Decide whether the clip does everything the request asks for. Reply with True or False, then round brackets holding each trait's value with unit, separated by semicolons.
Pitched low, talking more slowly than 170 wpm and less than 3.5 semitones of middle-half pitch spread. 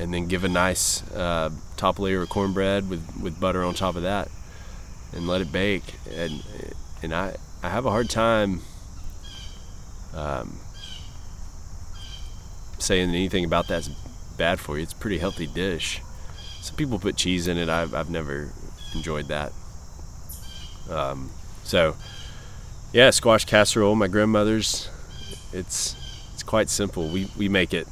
True (90 Hz; 145 wpm; 3.0 semitones)